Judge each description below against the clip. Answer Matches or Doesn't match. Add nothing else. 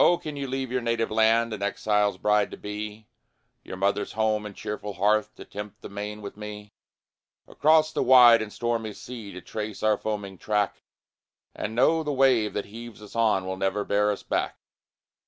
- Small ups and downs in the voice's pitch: Matches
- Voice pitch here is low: Matches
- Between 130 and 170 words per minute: Doesn't match